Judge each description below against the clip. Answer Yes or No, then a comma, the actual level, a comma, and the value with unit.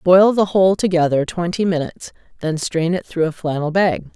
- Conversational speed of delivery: Yes, average, 190 wpm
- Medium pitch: Yes, medium, 175 Hz